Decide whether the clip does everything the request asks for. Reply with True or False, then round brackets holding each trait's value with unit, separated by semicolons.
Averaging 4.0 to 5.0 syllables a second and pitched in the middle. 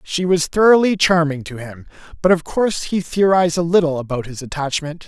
False (5.6 syllables/s; 165 Hz)